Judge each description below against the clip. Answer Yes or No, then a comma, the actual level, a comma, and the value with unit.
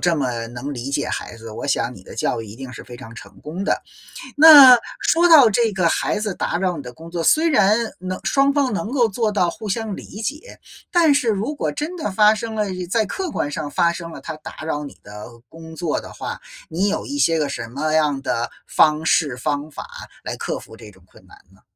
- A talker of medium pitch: Yes, medium, 170 Hz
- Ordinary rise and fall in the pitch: No, wide, 8.1 semitones